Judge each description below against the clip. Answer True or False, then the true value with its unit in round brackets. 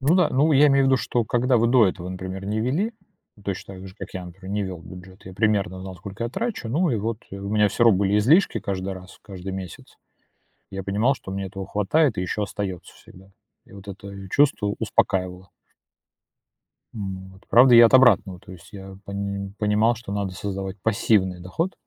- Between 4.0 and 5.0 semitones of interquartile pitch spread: False (3.6 semitones)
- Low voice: True (100 Hz)